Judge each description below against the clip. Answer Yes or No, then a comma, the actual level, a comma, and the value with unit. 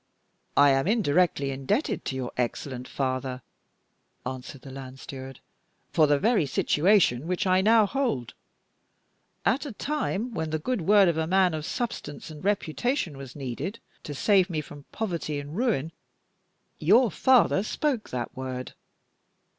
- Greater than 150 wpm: No, average, 145 wpm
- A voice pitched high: No, medium, 160 Hz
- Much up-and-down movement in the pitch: Yes, wide, 7.5 semitones